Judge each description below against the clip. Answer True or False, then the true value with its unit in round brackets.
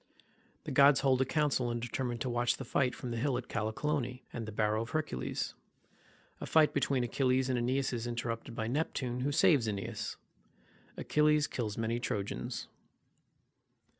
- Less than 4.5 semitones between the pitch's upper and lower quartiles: True (3.0 semitones)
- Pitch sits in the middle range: False (125 Hz)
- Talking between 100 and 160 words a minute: True (150 wpm)